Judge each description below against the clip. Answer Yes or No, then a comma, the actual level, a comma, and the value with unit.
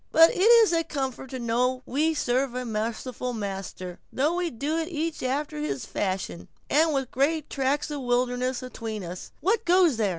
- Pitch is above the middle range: Yes, very high, 260 Hz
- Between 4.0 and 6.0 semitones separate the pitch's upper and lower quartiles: Yes, wide, 5.5 semitones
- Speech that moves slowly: No, average, 175 wpm